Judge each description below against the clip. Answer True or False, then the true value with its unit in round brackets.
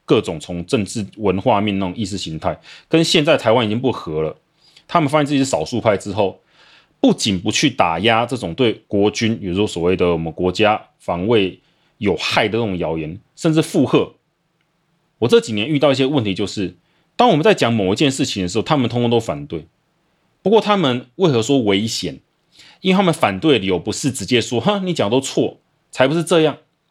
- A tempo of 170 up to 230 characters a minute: False (305 characters per minute)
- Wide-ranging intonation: True (8.4 semitones)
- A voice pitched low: True (125 Hz)